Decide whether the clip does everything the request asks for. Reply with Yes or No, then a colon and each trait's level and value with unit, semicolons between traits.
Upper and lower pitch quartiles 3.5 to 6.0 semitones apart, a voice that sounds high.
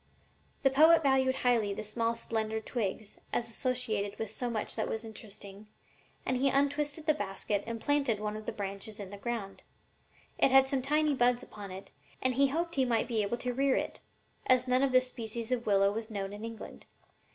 Yes: average, 3.8 semitones; high, 235 Hz